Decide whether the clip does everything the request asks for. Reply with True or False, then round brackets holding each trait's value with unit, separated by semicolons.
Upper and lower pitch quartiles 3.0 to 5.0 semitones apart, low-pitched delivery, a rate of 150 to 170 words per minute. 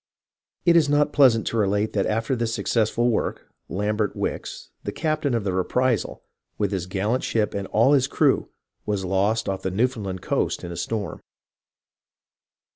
True (4.2 semitones; 110 Hz; 165 wpm)